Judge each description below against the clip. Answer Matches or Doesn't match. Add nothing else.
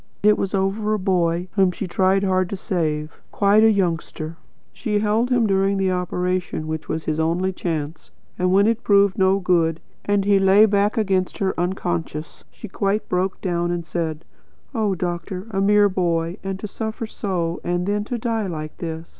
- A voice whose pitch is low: Doesn't match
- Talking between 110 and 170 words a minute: Doesn't match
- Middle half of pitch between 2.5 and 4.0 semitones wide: Matches